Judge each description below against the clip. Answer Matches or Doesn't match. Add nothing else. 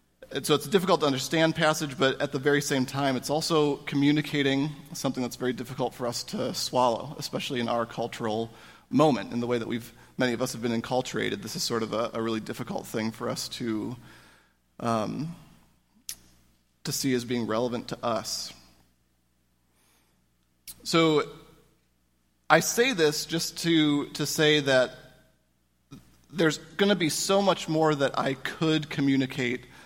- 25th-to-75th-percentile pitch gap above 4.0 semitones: Matches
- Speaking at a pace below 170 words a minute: Matches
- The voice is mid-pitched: Doesn't match